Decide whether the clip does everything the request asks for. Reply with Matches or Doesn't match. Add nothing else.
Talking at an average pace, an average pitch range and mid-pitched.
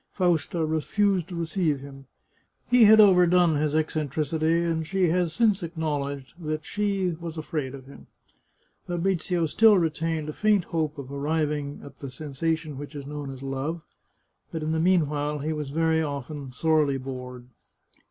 Matches